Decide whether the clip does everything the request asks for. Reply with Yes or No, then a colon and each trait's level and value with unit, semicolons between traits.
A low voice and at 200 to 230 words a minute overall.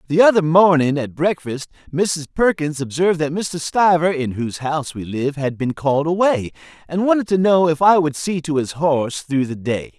No: medium, 160 Hz; fast, 205 wpm